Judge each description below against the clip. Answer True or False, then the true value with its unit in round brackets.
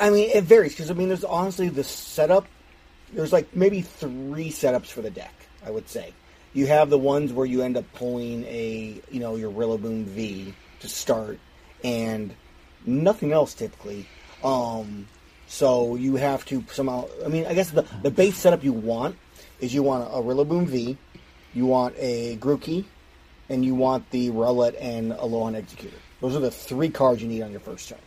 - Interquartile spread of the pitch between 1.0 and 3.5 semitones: False (4.7 semitones)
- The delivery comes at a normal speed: True (195 wpm)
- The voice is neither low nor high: False (125 Hz)